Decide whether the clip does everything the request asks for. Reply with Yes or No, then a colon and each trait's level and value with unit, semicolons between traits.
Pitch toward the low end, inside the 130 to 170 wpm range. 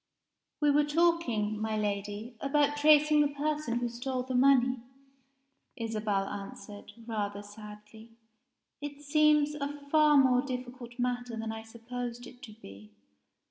No: high, 245 Hz; slow, 135 wpm